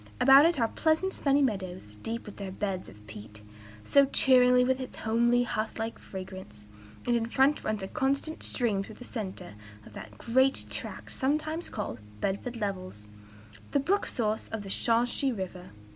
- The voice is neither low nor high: No, high, 230 Hz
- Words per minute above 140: Yes, average, 175 wpm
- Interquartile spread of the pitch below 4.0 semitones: No, wide, 5.6 semitones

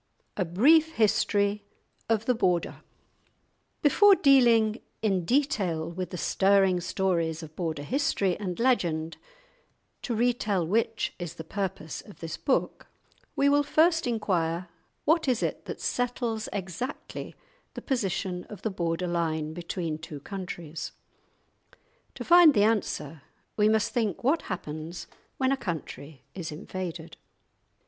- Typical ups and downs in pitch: No, wide, 6.0 semitones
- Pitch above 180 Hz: Yes, high, 190 Hz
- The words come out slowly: Yes, slow, 130 wpm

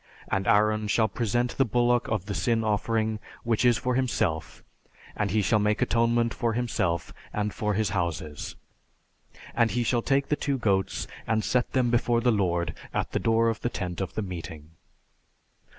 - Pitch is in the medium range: No, low, 110 Hz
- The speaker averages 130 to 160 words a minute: No, average, 180 wpm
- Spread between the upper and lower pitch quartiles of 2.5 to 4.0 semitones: Yes, average, 3.5 semitones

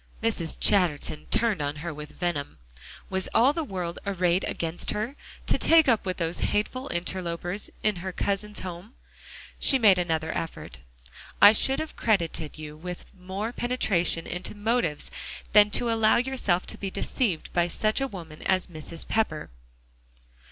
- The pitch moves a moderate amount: Yes, average, 4.4 semitones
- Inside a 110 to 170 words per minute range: Yes, average, 155 wpm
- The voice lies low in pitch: No, medium, 185 Hz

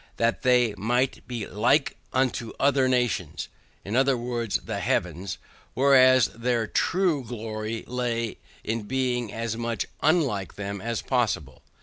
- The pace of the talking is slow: Yes, slow, 125 wpm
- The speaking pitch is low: Yes, low, 120 Hz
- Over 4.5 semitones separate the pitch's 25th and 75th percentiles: No, average, 2.7 semitones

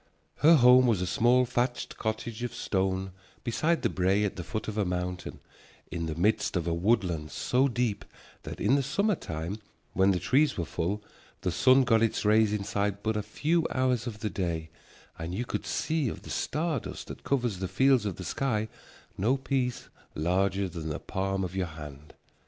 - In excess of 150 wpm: Yes, average, 195 wpm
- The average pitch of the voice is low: Yes, low, 105 Hz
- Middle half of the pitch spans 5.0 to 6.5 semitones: Yes, average, 5.3 semitones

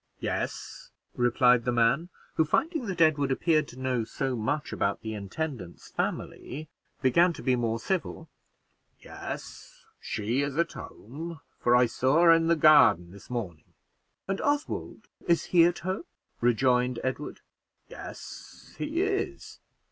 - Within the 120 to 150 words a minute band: Yes, average, 140 wpm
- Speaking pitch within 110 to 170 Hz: Yes, low, 135 Hz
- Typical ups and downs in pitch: No, wide, 5.7 semitones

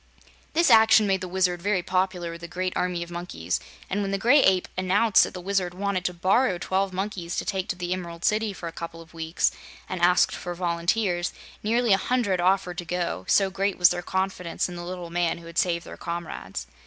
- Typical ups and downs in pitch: No, narrow, 2.1 semitones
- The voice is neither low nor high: Yes, medium, 180 Hz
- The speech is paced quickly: Yes, fast, 220 wpm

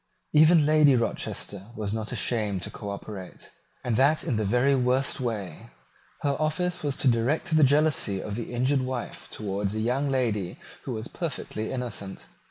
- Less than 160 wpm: No, average, 165 wpm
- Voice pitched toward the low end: Yes, low, 125 Hz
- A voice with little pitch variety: No, average, 4.9 semitones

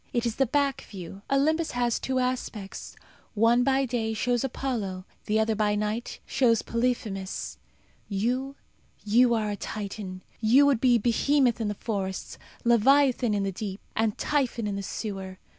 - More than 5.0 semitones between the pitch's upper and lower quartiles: No, average, 3.5 semitones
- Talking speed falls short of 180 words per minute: Yes, average, 160 wpm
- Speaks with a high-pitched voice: Yes, high, 230 Hz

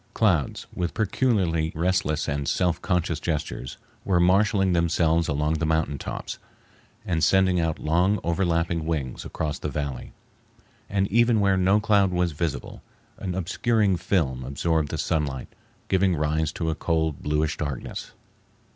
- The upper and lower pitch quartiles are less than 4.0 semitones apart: Yes, average, 3.5 semitones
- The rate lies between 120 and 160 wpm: Yes, average, 140 wpm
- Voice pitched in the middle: No, very low, 85 Hz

